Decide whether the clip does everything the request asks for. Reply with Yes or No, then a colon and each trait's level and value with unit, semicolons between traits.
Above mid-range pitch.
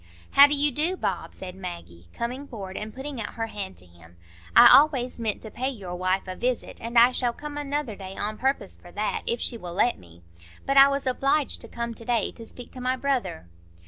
Yes: high, 235 Hz